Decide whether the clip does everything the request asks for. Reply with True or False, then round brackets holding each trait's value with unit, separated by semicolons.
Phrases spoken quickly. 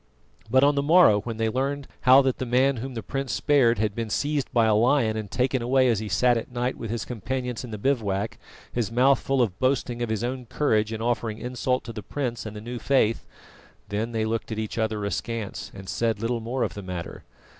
True (230 wpm)